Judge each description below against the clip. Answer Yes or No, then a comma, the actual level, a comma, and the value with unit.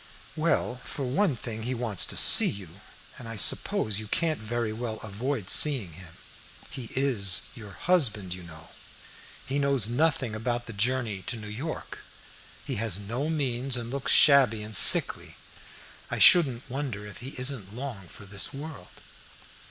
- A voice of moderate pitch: No, low, 120 Hz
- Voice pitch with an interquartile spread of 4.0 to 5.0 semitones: Yes, average, 4.6 semitones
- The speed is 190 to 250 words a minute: No, average, 160 wpm